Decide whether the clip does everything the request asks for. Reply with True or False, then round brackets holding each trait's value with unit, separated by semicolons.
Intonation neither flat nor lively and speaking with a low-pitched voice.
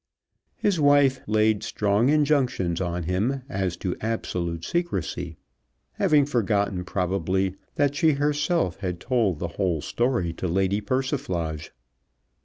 False (7.2 semitones; 100 Hz)